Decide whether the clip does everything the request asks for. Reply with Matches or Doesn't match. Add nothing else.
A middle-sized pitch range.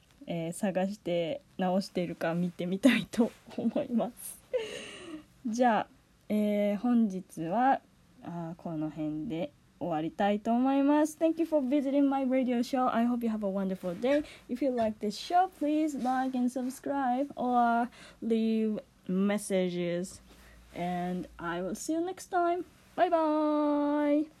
Doesn't match